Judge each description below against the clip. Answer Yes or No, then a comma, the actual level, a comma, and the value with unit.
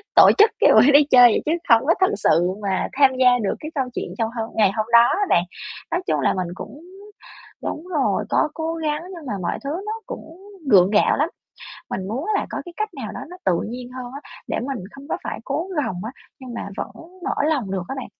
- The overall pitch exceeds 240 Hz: Yes, very high, 260 Hz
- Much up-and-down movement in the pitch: Yes, wide, 6.5 semitones